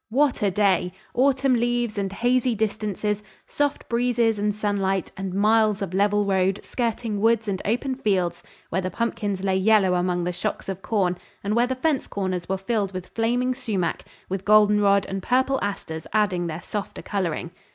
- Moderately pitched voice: No, high, 205 Hz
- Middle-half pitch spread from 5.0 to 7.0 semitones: No, average, 3.5 semitones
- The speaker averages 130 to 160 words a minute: No, average, 170 wpm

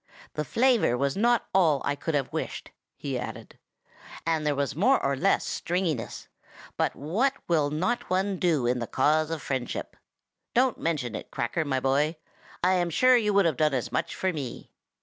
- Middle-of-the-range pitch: Yes, medium, 155 Hz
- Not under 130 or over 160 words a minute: No, average, 185 wpm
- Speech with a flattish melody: No, average, 5.3 semitones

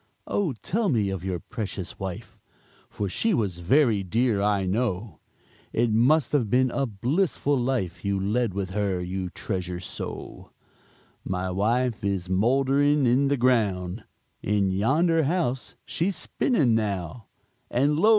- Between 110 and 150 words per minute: Yes, average, 140 wpm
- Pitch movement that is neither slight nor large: No, wide, 5.8 semitones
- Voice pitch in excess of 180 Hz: No, low, 110 Hz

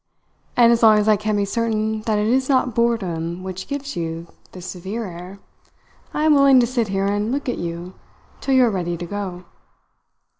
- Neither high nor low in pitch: No, high, 210 Hz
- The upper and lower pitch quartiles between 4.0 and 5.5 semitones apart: Yes, average, 4.5 semitones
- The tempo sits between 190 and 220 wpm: Yes, average, 200 wpm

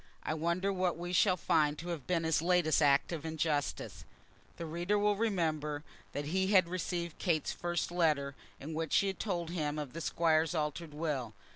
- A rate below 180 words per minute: No, average, 185 wpm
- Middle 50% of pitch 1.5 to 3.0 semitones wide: Yes, average, 2.7 semitones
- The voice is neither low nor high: Yes, medium, 165 Hz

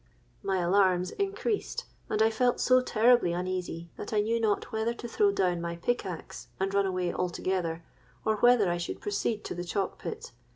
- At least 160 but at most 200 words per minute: Yes, average, 180 wpm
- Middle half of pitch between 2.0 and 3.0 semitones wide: No, average, 4.7 semitones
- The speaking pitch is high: Yes, high, 200 Hz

